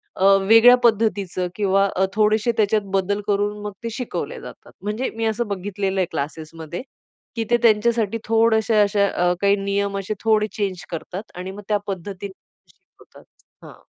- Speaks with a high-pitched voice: Yes, high, 205 Hz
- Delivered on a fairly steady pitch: Yes, narrow, 2.2 semitones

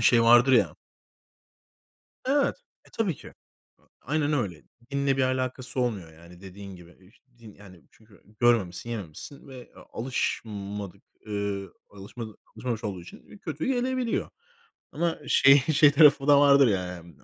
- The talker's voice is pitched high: No, low, 115 Hz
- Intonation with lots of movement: Yes, wide, 6.1 semitones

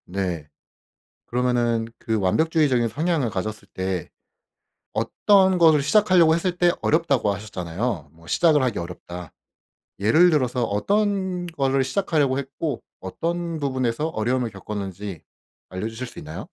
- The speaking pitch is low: Yes, low, 125 Hz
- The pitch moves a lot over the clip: Yes, wide, 8.2 semitones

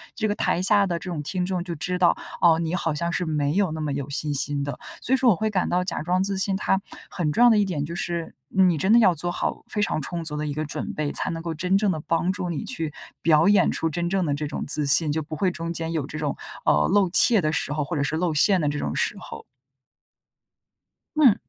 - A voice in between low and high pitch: Yes, medium, 170 Hz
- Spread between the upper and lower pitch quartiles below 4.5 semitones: Yes, average, 3.7 semitones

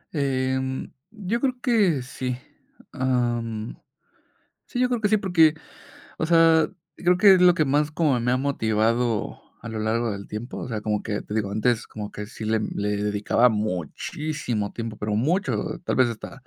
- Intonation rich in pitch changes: Yes, wide, 6.7 semitones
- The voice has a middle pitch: No, low, 125 Hz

